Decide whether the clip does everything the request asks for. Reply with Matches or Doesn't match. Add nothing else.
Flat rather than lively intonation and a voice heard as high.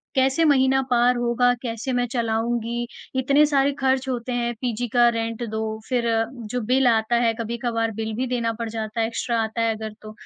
Matches